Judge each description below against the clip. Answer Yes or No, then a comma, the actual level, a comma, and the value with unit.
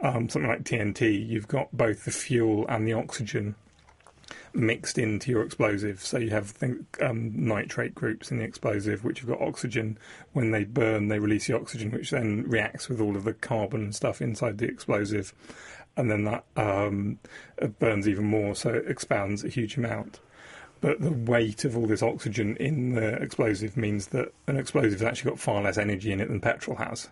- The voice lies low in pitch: Yes, low, 110 Hz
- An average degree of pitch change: No, narrow, 2.2 semitones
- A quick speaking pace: No, average, 195 wpm